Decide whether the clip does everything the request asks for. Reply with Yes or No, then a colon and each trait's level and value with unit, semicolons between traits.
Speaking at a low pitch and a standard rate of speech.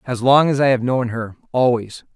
Yes: low, 125 Hz; average, 195 wpm